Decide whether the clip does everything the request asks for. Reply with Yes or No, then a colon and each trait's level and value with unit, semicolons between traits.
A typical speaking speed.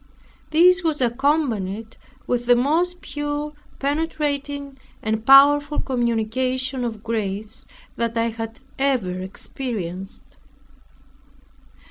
No: slow, 90 wpm